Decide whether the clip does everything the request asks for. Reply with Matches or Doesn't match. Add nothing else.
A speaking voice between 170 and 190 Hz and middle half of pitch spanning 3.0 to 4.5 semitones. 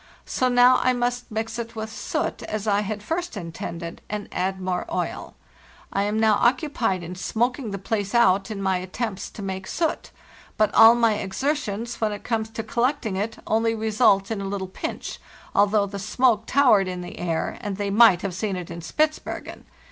Doesn't match